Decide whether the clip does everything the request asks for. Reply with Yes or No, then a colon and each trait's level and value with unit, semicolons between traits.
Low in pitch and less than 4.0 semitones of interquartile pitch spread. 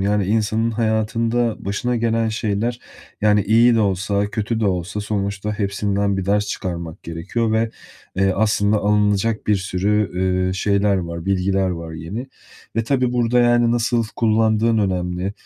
Yes: low, 105 Hz; narrow, 2.6 semitones